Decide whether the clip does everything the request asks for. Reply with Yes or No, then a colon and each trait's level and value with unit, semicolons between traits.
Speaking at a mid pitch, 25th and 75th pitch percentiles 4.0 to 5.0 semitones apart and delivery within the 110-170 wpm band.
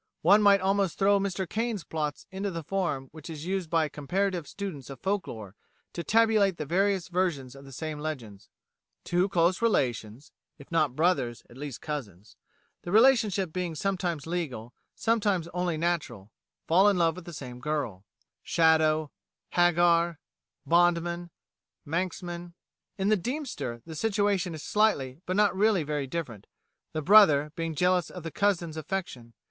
Yes: medium, 170 Hz; average, 4.6 semitones; average, 155 wpm